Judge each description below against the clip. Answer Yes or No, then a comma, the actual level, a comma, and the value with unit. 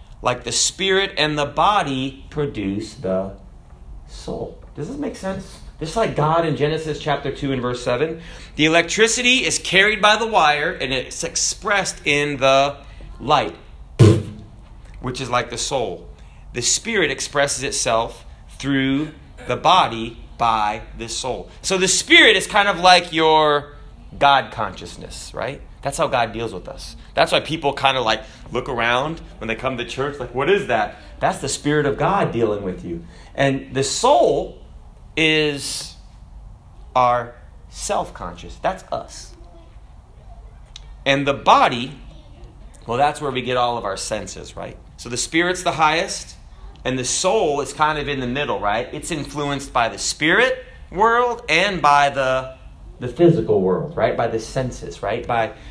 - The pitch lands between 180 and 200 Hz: No, low, 135 Hz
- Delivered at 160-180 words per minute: Yes, average, 165 wpm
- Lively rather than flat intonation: No, average, 4.8 semitones